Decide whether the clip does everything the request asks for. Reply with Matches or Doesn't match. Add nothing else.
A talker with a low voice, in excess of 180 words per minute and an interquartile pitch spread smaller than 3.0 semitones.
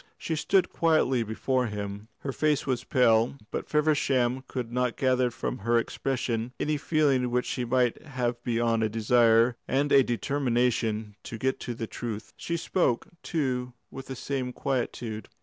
Doesn't match